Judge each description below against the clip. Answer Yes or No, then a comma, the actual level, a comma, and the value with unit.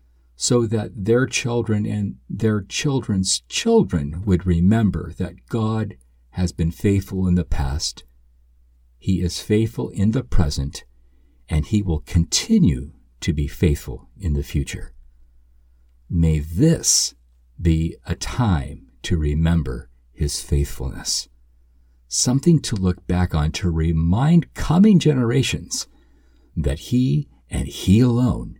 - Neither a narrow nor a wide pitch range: No, wide, 8.4 semitones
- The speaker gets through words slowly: Yes, slow, 120 wpm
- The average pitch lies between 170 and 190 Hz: No, very low, 85 Hz